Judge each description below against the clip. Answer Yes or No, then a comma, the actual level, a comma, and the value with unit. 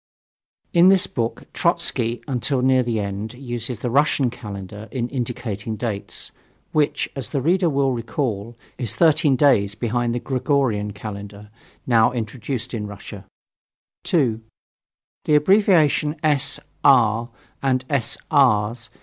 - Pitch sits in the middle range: No, low, 120 Hz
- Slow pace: Yes, slow, 125 wpm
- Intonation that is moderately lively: Yes, average, 4.3 semitones